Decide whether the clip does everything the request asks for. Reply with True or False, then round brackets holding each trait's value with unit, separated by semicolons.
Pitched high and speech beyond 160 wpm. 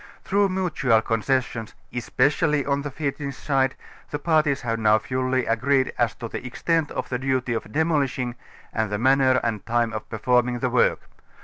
False (130 Hz; 170 wpm)